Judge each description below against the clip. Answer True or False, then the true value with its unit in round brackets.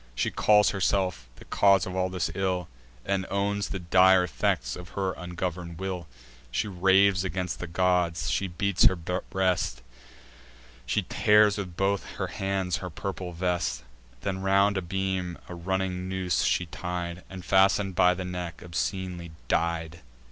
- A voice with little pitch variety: True (1.7 semitones)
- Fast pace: False (155 wpm)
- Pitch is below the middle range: True (90 Hz)